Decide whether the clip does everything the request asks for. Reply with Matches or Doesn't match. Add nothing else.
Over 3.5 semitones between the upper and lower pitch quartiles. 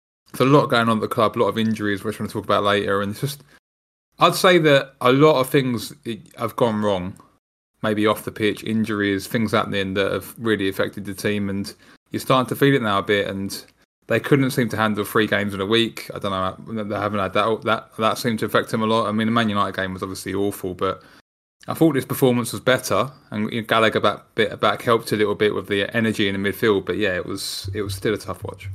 Doesn't match